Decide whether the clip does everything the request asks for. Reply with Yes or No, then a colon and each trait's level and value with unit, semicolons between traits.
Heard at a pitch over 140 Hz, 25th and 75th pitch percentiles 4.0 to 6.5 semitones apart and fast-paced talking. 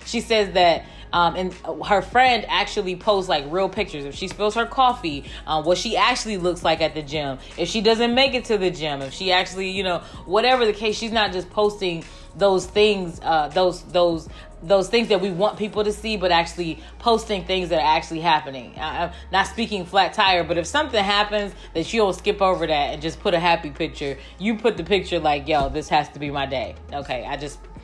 Yes: medium, 185 Hz; average, 4.4 semitones; fast, 220 wpm